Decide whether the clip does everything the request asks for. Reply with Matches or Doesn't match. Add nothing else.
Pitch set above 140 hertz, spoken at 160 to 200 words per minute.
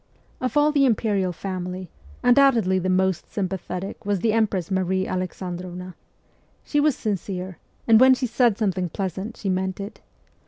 Doesn't match